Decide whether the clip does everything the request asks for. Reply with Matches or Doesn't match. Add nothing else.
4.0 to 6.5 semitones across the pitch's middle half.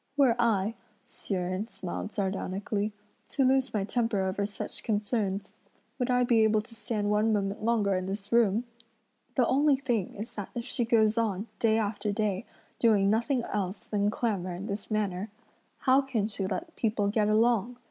Doesn't match